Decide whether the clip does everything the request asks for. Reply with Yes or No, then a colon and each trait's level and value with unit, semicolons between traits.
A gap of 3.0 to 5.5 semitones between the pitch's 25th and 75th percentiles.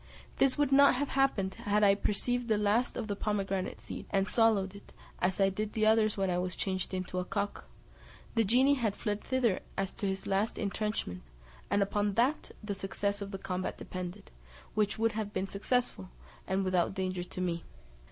No: narrow, 2.6 semitones